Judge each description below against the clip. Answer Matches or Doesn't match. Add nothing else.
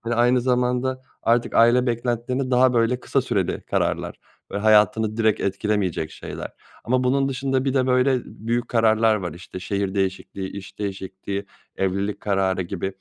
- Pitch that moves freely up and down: Doesn't match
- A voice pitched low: Matches